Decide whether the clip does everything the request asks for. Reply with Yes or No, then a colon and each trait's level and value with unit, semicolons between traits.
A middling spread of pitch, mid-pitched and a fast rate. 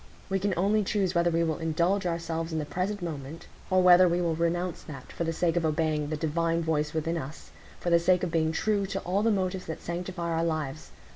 No: narrow, 2.2 semitones; medium, 170 Hz; fast, 225 wpm